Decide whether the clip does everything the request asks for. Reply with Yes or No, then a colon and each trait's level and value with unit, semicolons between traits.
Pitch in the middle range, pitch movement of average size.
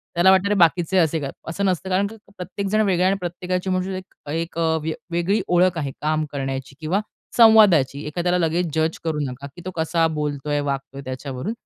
Yes: medium, 170 Hz; average, 3.7 semitones